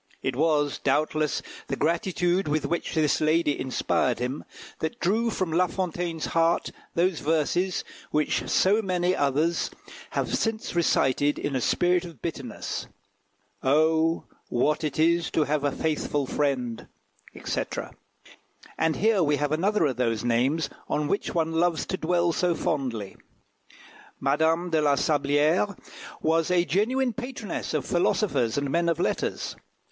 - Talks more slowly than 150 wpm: Yes, average, 140 wpm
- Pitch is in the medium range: Yes, medium, 160 Hz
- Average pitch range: Yes, average, 3.4 semitones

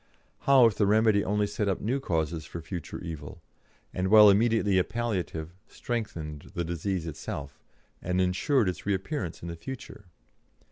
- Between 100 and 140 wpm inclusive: No, average, 160 wpm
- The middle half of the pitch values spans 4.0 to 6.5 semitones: Yes, average, 4.6 semitones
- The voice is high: No, very low, 95 Hz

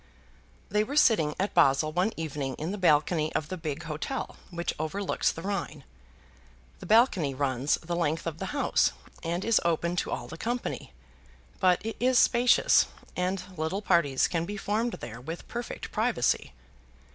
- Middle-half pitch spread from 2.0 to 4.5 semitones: No, average, 5.0 semitones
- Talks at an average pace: Yes, average, 165 wpm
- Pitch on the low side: No, medium, 170 Hz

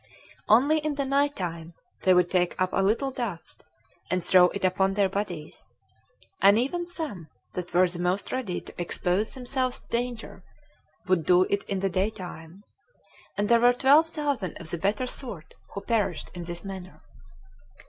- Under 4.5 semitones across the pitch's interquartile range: No, wide, 5.6 semitones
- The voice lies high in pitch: Yes, high, 195 Hz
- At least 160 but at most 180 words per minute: Yes, average, 175 wpm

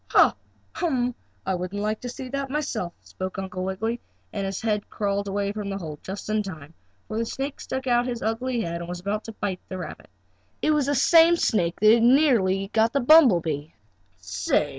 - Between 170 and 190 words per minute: No, average, 200 wpm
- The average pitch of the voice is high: Yes, high, 215 Hz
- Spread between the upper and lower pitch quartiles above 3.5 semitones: Yes, average, 4.8 semitones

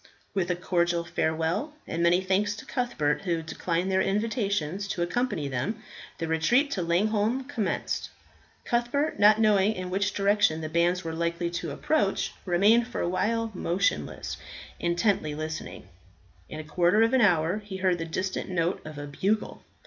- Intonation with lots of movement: No, average, 4.0 semitones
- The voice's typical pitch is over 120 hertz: Yes, medium, 185 Hz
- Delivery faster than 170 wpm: No, average, 165 wpm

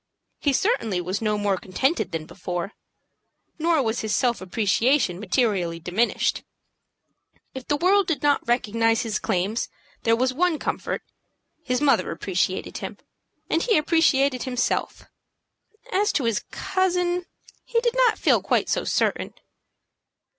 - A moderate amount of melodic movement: No, wide, 7.7 semitones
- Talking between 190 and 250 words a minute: No, slow, 135 wpm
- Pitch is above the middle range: Yes, very high, 250 Hz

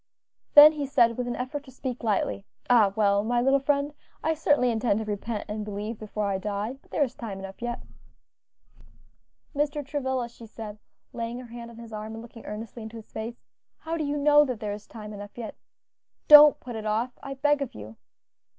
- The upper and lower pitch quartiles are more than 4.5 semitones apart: No, average, 4.2 semitones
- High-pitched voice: Yes, high, 235 Hz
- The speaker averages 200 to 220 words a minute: Yes, fast, 205 wpm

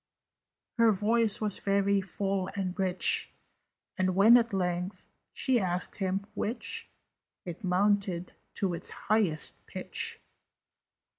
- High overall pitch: Yes, high, 195 Hz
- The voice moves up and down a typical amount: No, narrow, 2.3 semitones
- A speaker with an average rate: No, slow, 115 wpm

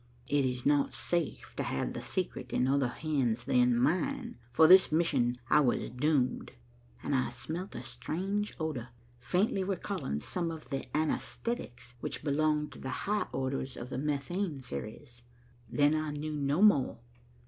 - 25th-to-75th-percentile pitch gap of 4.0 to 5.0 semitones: Yes, average, 4.7 semitones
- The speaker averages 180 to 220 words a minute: No, average, 160 wpm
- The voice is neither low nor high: Yes, medium, 145 Hz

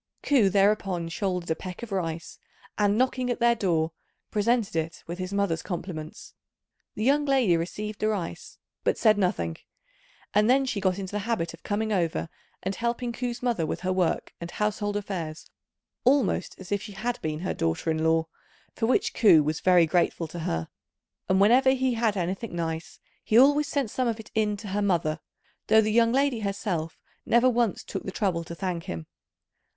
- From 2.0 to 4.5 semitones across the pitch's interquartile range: No, average, 5.3 semitones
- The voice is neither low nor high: No, high, 200 Hz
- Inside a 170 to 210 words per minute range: Yes, average, 190 wpm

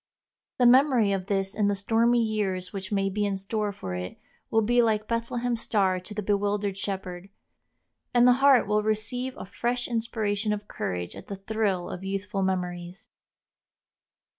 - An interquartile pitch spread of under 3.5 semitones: Yes, average, 3.0 semitones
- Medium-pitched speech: No, high, 205 Hz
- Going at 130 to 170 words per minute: Yes, average, 165 wpm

